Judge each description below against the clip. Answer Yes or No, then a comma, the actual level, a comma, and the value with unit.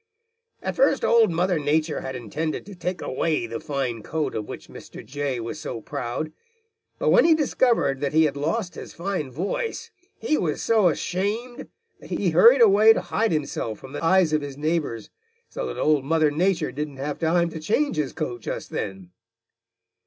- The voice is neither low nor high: Yes, medium, 160 Hz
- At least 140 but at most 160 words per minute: No, average, 185 wpm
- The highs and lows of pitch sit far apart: Yes, wide, 5.7 semitones